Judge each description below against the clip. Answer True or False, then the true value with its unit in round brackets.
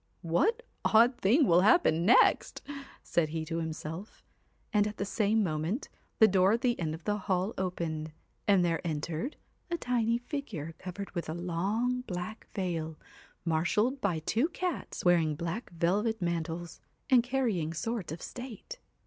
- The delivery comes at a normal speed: True (160 wpm)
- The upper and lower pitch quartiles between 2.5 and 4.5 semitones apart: False (5.6 semitones)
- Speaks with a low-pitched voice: False (185 Hz)